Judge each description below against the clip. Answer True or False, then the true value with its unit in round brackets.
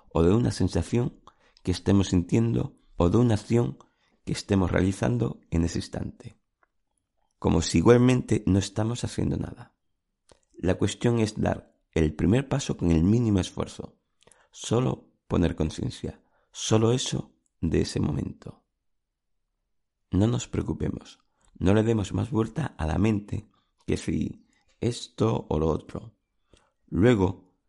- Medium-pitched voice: False (100 Hz)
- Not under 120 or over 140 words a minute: True (130 wpm)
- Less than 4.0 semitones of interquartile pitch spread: False (4.3 semitones)